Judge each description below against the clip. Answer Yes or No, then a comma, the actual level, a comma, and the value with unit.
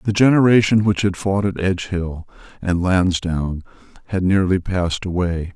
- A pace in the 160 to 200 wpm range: No, average, 140 wpm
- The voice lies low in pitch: Yes, very low, 95 Hz